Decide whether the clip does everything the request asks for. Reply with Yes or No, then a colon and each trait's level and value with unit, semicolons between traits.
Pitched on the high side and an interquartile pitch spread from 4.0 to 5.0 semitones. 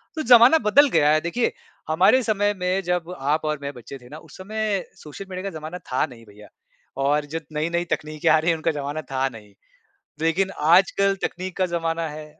No: medium, 165 Hz; average, 4.3 semitones